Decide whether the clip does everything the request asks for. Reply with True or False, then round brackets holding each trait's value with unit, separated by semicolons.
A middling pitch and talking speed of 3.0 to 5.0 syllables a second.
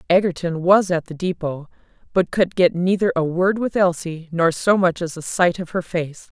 True (175 Hz; 4.8 syllables/s)